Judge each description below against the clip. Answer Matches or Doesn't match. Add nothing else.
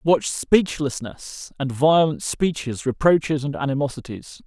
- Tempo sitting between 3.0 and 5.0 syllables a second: Matches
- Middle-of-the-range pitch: Matches